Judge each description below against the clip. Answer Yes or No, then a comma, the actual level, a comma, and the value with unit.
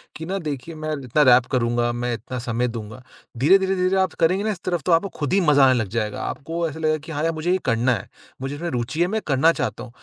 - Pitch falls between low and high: Yes, medium, 150 Hz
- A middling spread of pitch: No, wide, 5.7 semitones